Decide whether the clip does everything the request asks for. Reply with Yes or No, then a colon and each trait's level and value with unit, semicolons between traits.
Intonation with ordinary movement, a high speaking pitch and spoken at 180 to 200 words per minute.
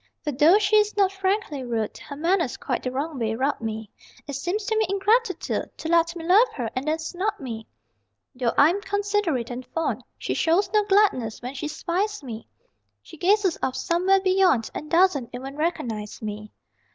No: wide, 7.2 semitones; very high, 325 Hz; average, 185 wpm